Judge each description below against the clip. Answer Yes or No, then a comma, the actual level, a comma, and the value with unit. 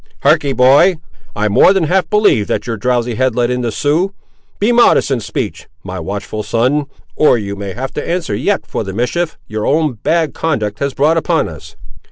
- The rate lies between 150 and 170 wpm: No, average, 200 wpm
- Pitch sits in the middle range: No, low, 125 Hz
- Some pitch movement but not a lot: No, wide, 7.2 semitones